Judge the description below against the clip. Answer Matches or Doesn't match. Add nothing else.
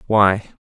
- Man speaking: Matches